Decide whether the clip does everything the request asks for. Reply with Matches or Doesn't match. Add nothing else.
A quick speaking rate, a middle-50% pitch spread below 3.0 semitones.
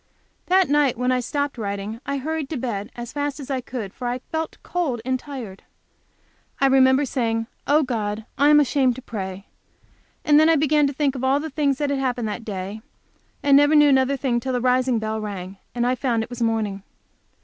Doesn't match